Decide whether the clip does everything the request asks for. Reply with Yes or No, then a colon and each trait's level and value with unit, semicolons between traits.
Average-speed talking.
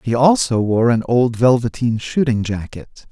Yes: average, 155 wpm